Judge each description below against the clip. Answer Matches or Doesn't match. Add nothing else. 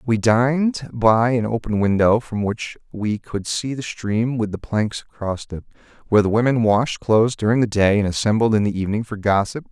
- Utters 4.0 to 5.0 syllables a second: Doesn't match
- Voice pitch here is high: Doesn't match